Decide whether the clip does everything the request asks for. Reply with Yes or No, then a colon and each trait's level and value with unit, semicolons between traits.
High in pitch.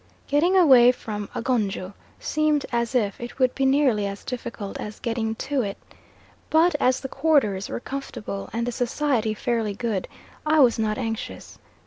Yes: high, 240 Hz